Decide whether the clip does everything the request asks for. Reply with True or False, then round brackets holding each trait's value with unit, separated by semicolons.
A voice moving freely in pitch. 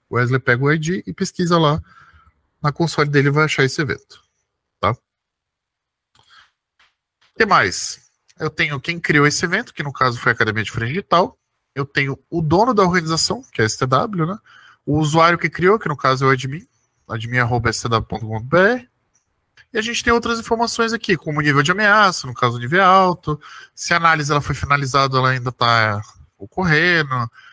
True (5.7 semitones)